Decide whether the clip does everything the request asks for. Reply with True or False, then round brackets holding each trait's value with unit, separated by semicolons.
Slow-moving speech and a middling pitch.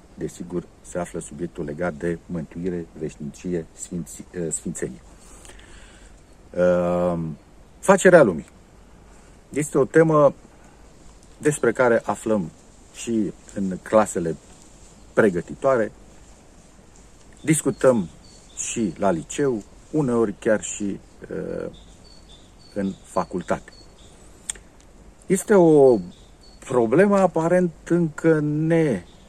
False (80 wpm; 105 Hz)